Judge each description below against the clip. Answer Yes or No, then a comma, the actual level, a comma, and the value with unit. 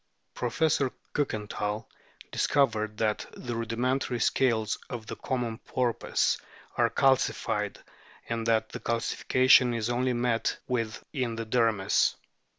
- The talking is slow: Yes, slow, 120 wpm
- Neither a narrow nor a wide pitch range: No, narrow, 2.3 semitones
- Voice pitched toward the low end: Yes, low, 115 Hz